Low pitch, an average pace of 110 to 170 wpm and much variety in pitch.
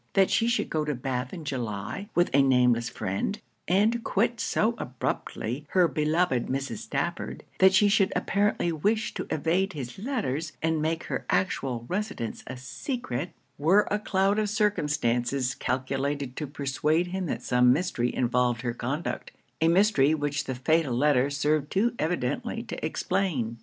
No: medium, 150 Hz; average, 155 wpm; wide, 6.9 semitones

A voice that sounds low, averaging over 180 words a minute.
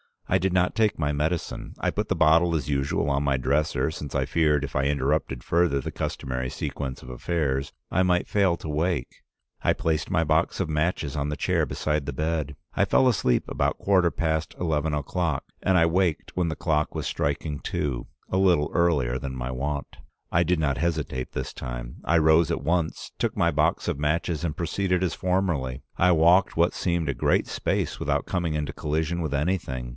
Yes: very low, 80 Hz; average, 200 wpm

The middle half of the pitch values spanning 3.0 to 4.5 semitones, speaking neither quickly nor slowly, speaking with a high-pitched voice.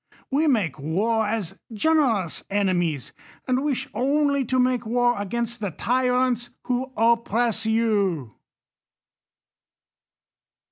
No: average, 3.8 semitones; slow, 100 wpm; high, 230 Hz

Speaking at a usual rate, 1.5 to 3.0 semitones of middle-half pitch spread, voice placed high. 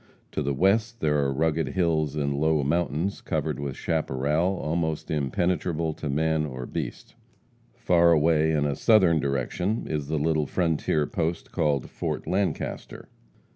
No: average, 145 wpm; narrow, 2.6 semitones; very low, 80 Hz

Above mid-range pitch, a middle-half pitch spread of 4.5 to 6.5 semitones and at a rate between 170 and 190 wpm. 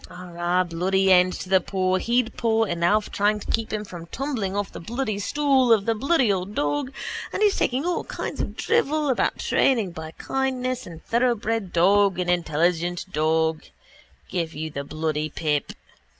Yes: high, 195 Hz; wide, 5.6 semitones; average, 180 wpm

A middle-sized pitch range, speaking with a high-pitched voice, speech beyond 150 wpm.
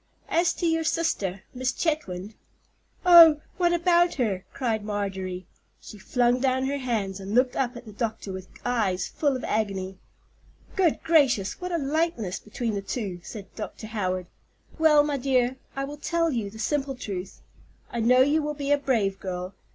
No: wide, 6.7 semitones; high, 245 Hz; average, 175 wpm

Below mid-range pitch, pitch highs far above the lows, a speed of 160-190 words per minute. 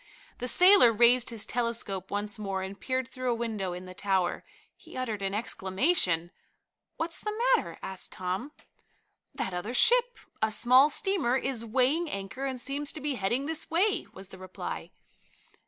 No: high, 235 Hz; wide, 6.2 semitones; average, 165 wpm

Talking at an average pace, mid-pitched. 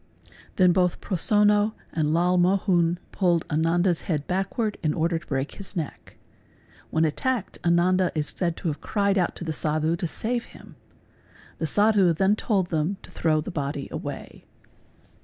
Yes: average, 160 wpm; medium, 175 Hz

